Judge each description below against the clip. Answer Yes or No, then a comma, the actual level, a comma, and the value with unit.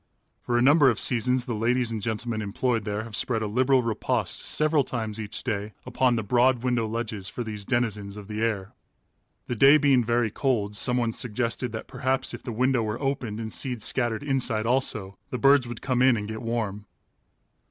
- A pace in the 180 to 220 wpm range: Yes, average, 195 wpm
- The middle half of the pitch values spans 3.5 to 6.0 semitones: No, average, 2.8 semitones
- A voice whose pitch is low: Yes, low, 115 Hz